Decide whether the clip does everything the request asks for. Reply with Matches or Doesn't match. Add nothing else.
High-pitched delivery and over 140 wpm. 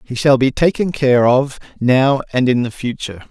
Doesn't match